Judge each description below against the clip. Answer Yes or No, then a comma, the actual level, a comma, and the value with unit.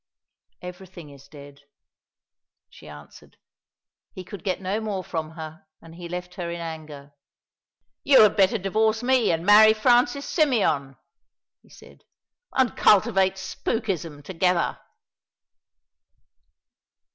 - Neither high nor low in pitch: Yes, medium, 180 Hz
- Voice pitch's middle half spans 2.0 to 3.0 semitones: No, average, 5.1 semitones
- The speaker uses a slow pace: Yes, slow, 115 wpm